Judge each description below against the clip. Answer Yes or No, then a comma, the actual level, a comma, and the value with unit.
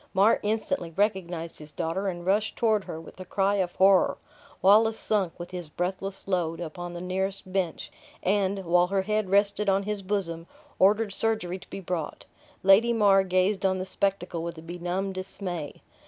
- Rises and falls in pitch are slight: Yes, narrow, 2.3 semitones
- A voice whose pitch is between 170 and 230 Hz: Yes, high, 190 Hz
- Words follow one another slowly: No, average, 175 wpm